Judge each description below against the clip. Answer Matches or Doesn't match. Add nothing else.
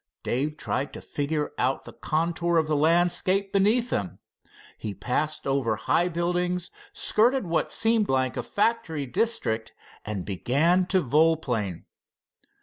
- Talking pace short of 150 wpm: Matches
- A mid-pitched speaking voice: Matches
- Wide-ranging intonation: Matches